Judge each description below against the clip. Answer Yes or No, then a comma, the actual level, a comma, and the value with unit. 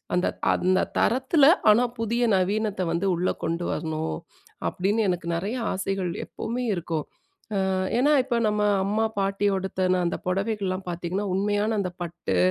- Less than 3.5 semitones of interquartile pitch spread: Yes, average, 3.1 semitones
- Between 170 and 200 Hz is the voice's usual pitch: Yes, high, 195 Hz